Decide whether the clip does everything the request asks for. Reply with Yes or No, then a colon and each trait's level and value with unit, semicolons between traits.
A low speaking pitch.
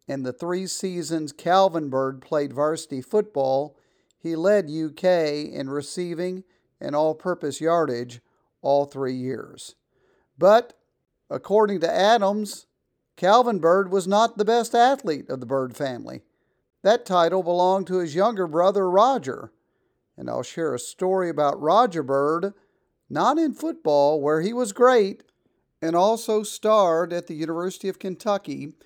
No: medium, 175 Hz